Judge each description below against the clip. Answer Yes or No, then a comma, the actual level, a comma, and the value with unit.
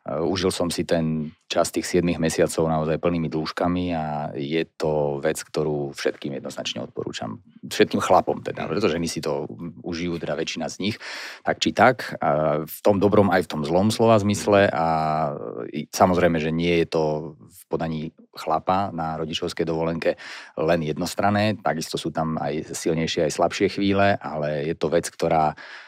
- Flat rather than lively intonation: Yes, narrow, 2.1 semitones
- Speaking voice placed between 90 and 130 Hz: No, very low, 80 Hz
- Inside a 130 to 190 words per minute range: Yes, average, 160 wpm